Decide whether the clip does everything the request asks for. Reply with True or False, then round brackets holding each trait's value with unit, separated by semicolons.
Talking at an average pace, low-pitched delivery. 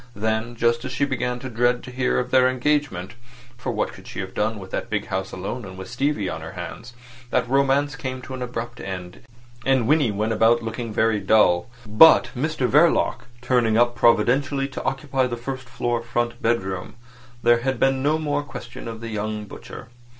True (195 wpm; 120 Hz)